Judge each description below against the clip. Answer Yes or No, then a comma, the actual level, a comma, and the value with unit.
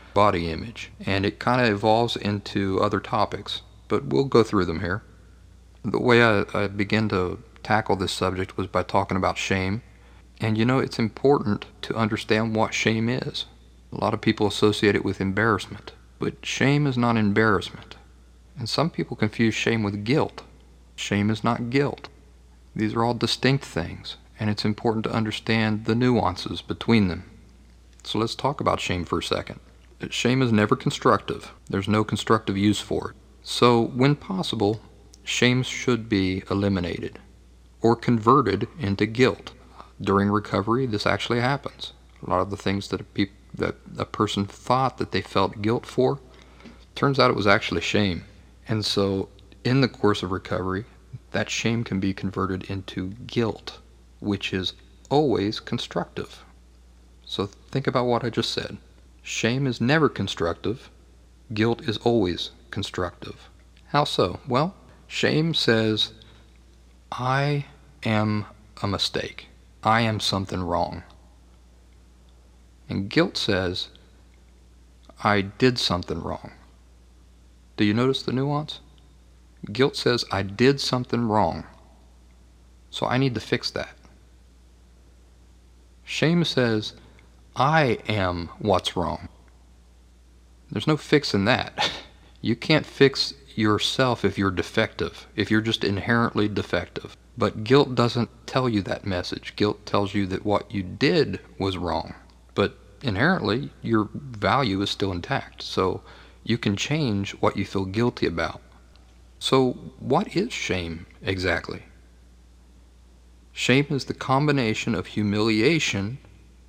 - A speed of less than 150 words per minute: Yes, average, 140 wpm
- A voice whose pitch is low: Yes, low, 100 Hz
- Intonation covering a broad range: Yes, wide, 8.1 semitones